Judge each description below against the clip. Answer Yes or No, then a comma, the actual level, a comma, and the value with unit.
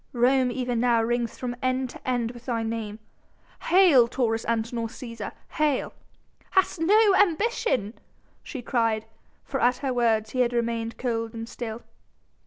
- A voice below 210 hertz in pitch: No, high, 240 Hz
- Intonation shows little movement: Yes, narrow, 2.3 semitones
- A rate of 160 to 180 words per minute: No, average, 150 wpm